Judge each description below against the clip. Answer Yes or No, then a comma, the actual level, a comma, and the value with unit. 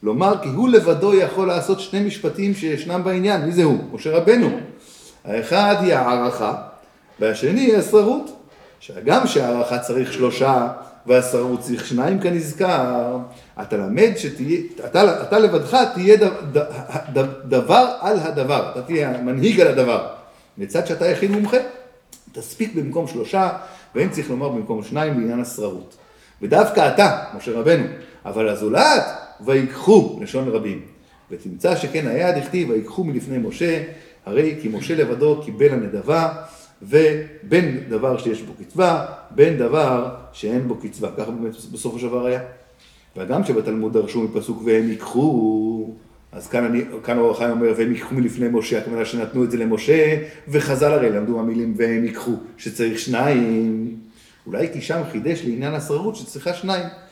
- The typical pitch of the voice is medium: Yes, medium, 145 Hz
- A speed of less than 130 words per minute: No, average, 140 wpm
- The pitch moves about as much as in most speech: No, wide, 7.6 semitones